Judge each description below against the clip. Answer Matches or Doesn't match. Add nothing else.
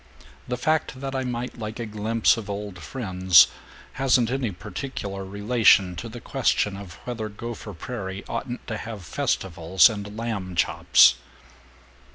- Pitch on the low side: Matches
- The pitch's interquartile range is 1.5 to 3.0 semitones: Doesn't match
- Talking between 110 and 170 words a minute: Matches